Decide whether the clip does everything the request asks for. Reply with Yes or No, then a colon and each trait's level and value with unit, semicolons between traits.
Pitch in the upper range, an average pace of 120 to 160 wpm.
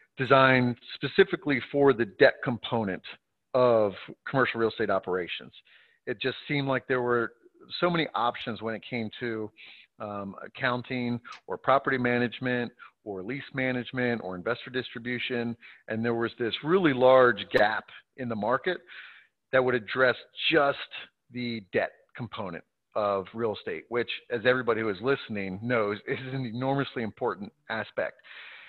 No: low, 125 Hz; average, 140 wpm